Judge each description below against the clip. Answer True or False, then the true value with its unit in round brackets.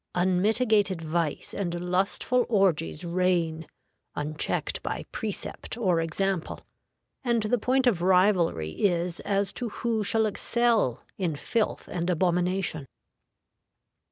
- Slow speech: True (110 wpm)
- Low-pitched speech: False (185 Hz)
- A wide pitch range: False (4.0 semitones)